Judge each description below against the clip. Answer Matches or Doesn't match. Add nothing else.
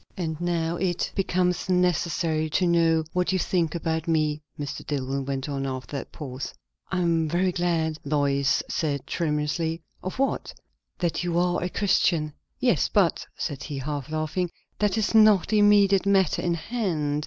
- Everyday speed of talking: Matches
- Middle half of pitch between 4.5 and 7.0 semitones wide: Doesn't match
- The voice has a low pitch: Doesn't match